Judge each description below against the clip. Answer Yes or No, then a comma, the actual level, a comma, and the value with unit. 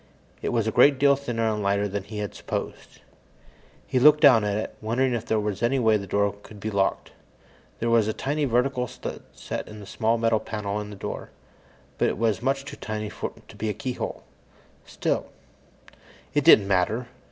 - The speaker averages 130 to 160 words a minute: No, average, 195 wpm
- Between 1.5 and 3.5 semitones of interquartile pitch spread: Yes, average, 3.2 semitones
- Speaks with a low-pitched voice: Yes, low, 110 Hz